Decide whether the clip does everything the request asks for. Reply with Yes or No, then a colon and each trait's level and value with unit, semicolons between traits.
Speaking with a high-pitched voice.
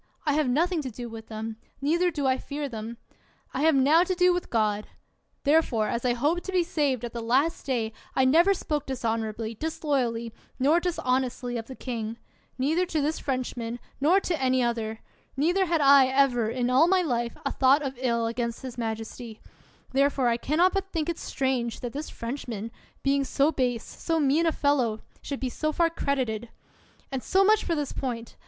Yes: very high, 265 Hz